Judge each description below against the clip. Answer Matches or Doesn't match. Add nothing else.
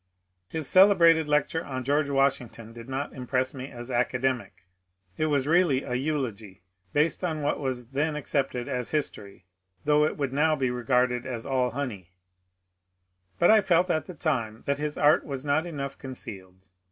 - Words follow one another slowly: Doesn't match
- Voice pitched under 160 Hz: Matches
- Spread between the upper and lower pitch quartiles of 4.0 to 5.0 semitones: Doesn't match